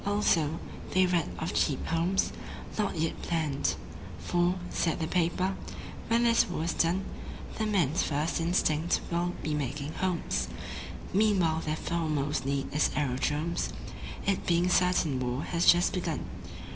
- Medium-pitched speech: Yes, medium, 170 Hz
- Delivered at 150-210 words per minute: No, average, 140 wpm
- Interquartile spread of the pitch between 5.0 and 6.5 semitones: No, average, 3.1 semitones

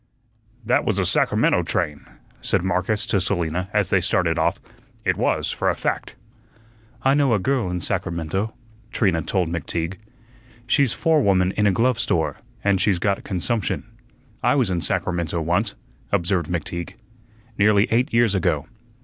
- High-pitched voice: No, very low, 95 Hz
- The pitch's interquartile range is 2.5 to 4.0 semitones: Yes, average, 3.7 semitones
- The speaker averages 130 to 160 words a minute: Yes, average, 150 wpm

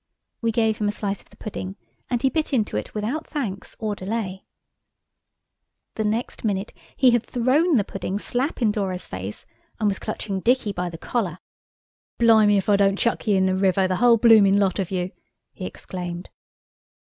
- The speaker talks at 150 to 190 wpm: Yes, average, 185 wpm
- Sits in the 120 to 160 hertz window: No, high, 205 Hz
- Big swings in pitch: No, average, 3.5 semitones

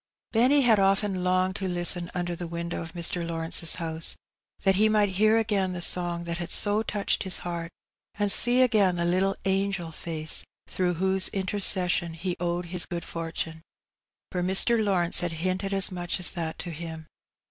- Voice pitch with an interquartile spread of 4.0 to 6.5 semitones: No, narrow, 2.4 semitones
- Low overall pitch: No, medium, 180 Hz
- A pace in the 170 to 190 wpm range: Yes, average, 180 wpm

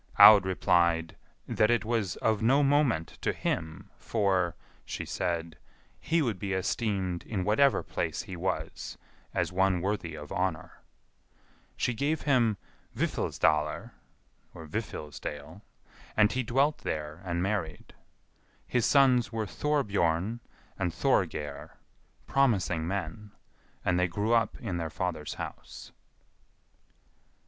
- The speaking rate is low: Yes, slow, 120 wpm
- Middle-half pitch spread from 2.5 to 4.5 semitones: No, average, 5.2 semitones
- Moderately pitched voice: No, very low, 95 Hz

